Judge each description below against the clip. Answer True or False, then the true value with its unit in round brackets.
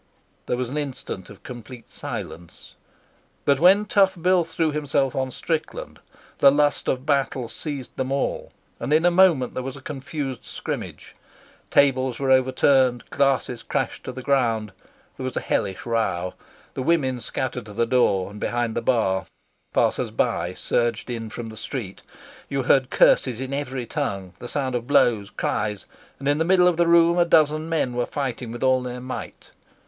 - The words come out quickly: False (175 wpm)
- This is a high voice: False (130 Hz)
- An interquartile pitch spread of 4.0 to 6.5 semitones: False (3.5 semitones)